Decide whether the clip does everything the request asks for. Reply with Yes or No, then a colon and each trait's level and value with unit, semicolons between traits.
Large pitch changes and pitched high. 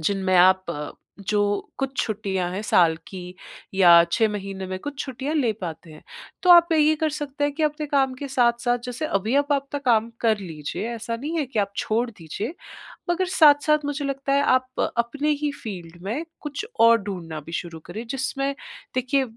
Yes: wide, 6.9 semitones; high, 240 Hz